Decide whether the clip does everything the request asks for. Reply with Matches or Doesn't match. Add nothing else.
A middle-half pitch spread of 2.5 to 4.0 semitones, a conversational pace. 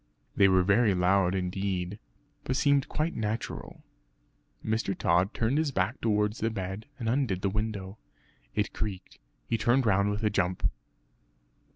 Matches